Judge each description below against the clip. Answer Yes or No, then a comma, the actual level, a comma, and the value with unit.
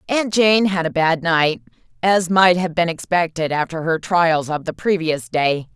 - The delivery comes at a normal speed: Yes, average, 190 wpm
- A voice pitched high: No, medium, 170 Hz